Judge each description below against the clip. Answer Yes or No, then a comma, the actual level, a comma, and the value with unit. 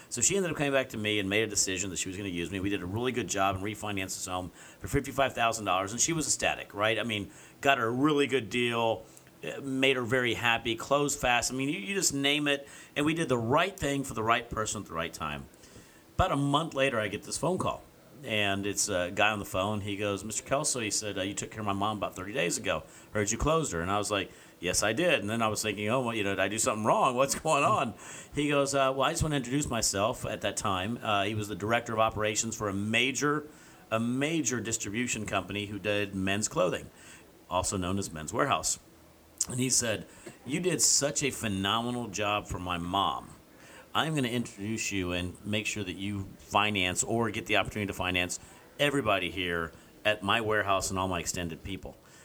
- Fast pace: Yes, fast, 240 wpm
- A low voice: Yes, low, 110 Hz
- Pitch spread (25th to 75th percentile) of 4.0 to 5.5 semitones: Yes, average, 4.9 semitones